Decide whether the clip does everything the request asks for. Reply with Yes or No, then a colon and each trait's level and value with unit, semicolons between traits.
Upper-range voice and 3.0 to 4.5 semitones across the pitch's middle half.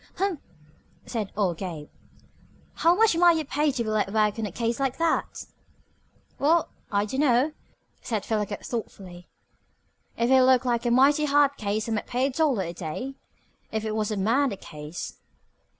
No: high, 235 Hz; average, 5.3 semitones